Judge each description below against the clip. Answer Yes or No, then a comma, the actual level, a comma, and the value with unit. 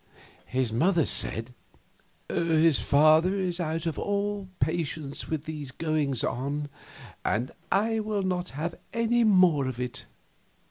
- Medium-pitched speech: Yes, medium, 160 Hz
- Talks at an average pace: No, slow, 125 wpm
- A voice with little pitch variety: No, average, 5.0 semitones